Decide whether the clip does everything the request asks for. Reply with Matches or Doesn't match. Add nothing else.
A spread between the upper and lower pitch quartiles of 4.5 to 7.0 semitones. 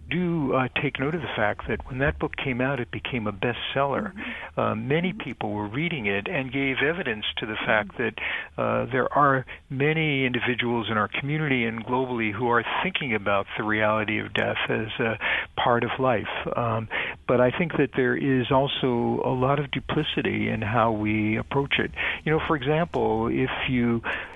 Doesn't match